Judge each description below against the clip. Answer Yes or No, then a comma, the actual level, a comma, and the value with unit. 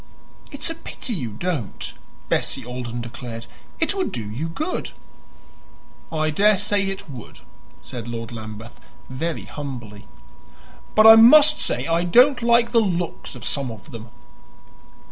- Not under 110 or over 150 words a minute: Yes, average, 140 wpm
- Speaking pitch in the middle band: Yes, medium, 155 Hz